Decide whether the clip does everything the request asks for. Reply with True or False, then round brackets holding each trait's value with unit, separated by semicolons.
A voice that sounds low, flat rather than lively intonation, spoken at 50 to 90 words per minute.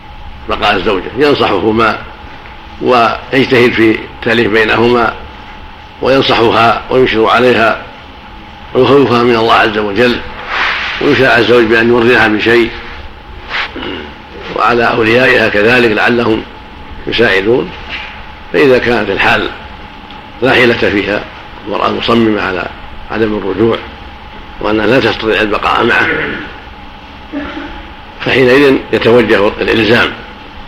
True (115 Hz; 1.8 semitones; 85 wpm)